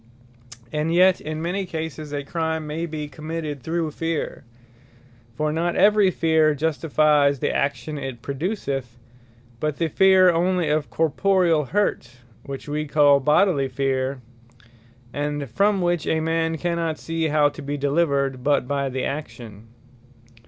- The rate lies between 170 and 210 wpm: No, average, 140 wpm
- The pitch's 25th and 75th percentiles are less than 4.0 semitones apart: Yes, average, 2.8 semitones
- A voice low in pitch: No, medium, 155 Hz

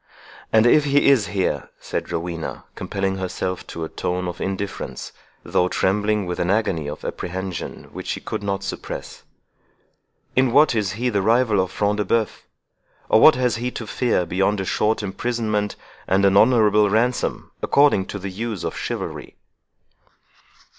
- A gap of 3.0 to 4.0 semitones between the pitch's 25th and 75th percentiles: Yes, average, 3.4 semitones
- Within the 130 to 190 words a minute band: Yes, average, 160 wpm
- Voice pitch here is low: Yes, low, 105 Hz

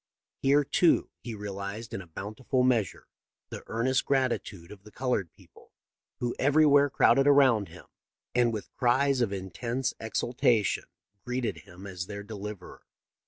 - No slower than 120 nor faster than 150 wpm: Yes, average, 140 wpm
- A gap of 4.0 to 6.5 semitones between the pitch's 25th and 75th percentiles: Yes, average, 4.7 semitones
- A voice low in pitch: Yes, low, 115 Hz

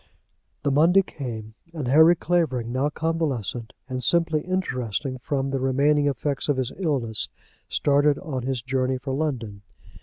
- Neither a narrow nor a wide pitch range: Yes, average, 3.2 semitones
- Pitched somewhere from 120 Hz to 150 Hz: Yes, low, 135 Hz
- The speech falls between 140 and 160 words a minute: Yes, average, 145 wpm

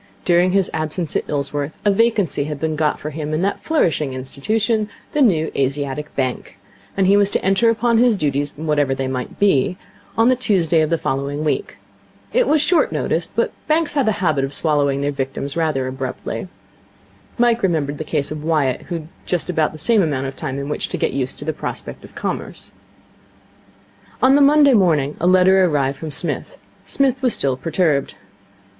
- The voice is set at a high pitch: No, medium, 160 Hz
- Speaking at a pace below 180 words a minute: No, average, 195 wpm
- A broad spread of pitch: Yes, wide, 6.1 semitones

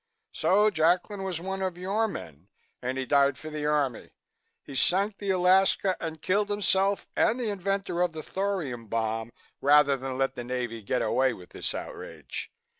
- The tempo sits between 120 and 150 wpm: No, average, 175 wpm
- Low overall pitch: No, medium, 160 Hz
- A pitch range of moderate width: No, wide, 6.8 semitones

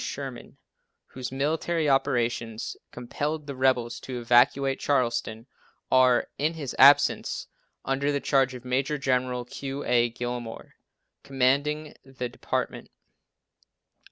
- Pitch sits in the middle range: No, low, 130 Hz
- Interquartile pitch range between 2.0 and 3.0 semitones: Yes, narrow, 2.4 semitones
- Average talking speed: No, slow, 110 wpm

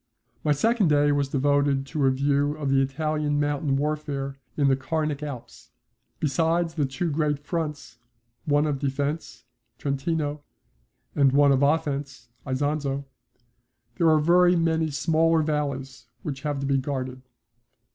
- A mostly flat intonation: Yes, narrow, 2.0 semitones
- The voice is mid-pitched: Yes, medium, 145 Hz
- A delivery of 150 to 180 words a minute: No, average, 140 wpm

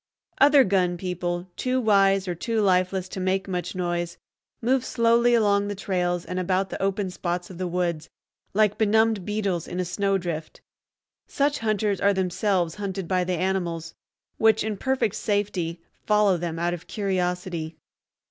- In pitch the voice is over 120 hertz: Yes, high, 190 Hz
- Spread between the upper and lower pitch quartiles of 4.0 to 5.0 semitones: No, average, 2.8 semitones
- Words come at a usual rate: Yes, average, 155 wpm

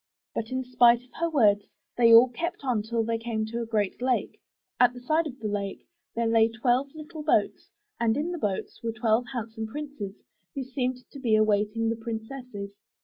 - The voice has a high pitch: Yes, high, 235 Hz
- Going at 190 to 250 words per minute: Yes, average, 200 wpm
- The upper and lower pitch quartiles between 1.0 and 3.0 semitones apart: Yes, average, 2.7 semitones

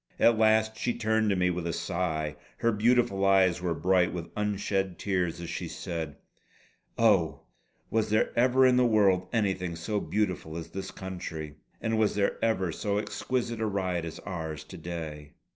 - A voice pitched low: Yes, very low, 95 Hz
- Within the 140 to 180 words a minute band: Yes, average, 175 wpm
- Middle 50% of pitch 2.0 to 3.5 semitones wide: No, average, 4.2 semitones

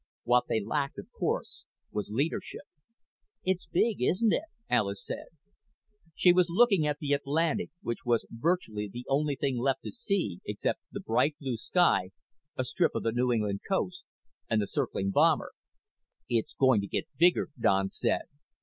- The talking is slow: No, average, 165 wpm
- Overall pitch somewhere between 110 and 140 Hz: Yes, low, 135 Hz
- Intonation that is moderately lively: No, wide, 7.2 semitones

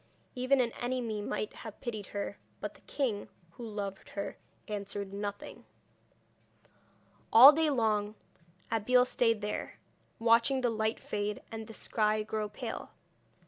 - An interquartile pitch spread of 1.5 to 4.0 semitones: Yes, average, 2.7 semitones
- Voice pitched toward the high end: Yes, high, 220 Hz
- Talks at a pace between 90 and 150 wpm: Yes, slow, 135 wpm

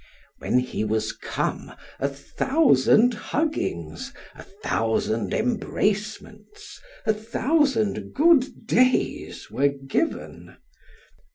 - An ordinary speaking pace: No, slow, 85 wpm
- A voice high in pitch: Yes, high, 215 Hz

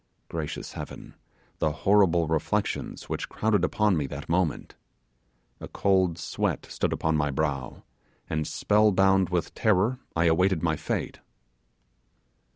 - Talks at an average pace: No, slow, 130 wpm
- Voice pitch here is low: Yes, very low, 85 Hz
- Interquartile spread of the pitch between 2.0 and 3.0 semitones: No, average, 3.8 semitones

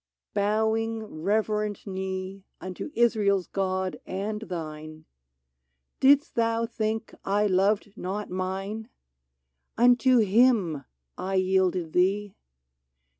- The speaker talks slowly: Yes, slow, 105 wpm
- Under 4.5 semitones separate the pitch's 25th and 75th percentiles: Yes, average, 2.9 semitones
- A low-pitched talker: No, high, 200 Hz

